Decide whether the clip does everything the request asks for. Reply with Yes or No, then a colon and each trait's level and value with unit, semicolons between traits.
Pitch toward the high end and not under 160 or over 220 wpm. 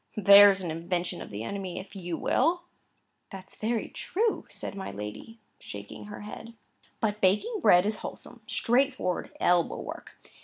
No: high, 200 Hz; average, 150 wpm